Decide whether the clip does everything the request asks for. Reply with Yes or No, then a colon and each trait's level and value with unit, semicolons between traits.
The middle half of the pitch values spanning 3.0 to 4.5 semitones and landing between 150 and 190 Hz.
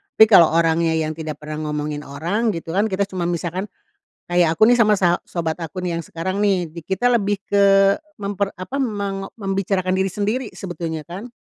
Yes: average, 3.4 semitones; medium, 185 Hz